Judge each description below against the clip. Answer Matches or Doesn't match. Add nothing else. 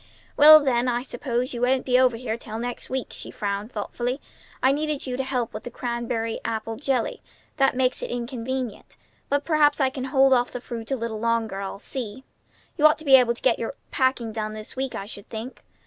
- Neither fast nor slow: Doesn't match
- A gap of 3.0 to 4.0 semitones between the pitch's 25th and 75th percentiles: Doesn't match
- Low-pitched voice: Doesn't match